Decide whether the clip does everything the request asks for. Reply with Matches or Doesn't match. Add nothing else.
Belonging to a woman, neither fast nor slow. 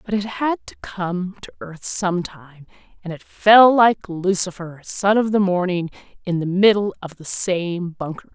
Matches